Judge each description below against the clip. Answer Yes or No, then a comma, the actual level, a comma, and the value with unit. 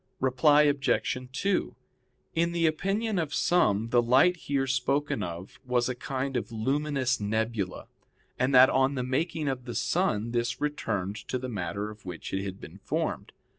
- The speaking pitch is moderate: No, low, 130 Hz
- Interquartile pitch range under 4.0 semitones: No, average, 4.7 semitones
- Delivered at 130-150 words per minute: No, average, 170 wpm